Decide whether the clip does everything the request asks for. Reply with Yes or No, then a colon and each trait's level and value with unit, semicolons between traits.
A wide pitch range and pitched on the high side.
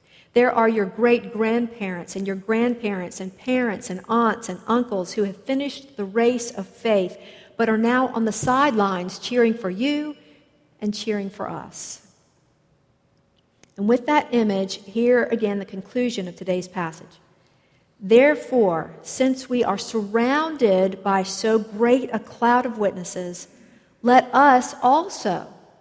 No: average, 4.0 semitones; high, 225 Hz